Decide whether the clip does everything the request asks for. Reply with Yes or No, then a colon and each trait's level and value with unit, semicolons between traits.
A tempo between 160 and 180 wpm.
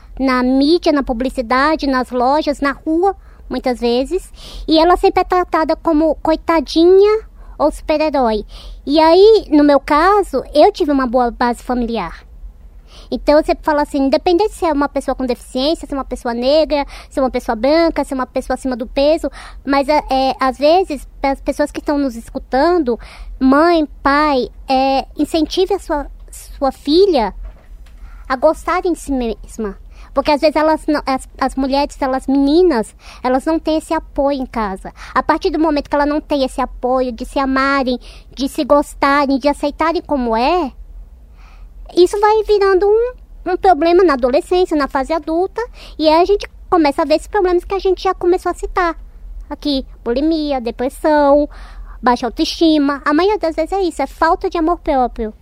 Yes: average, 175 wpm